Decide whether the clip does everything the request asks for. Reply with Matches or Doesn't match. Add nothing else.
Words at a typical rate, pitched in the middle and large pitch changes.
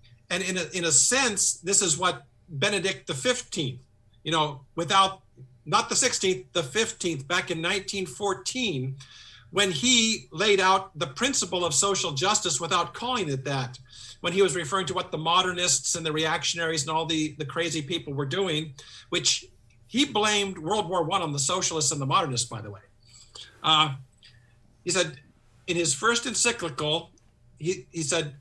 Matches